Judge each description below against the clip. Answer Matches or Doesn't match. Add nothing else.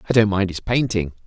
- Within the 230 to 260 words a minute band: Matches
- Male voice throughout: Matches